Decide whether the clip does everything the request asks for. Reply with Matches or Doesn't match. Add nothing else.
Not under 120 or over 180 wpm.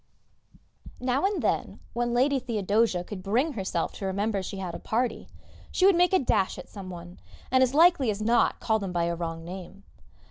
Doesn't match